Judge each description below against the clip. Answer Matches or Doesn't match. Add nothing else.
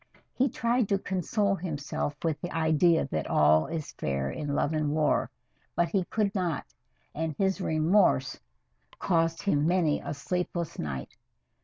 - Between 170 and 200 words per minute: Doesn't match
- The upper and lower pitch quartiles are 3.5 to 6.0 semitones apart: Matches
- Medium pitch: Matches